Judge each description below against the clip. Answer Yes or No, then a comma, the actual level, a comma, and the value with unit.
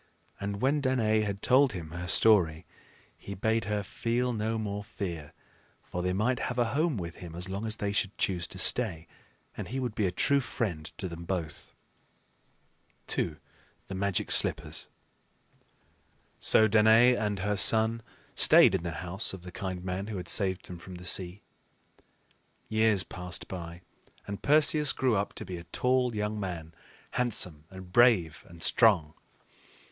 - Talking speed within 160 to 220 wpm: Yes, average, 165 wpm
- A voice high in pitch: No, low, 100 Hz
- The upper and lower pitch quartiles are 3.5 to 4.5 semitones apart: Yes, average, 3.9 semitones